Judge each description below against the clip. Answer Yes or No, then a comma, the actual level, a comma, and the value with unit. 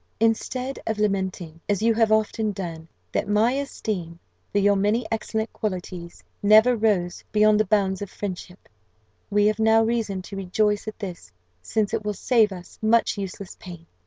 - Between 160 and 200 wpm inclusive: Yes, average, 165 wpm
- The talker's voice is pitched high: Yes, high, 210 Hz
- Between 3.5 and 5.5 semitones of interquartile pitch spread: No, average, 2.7 semitones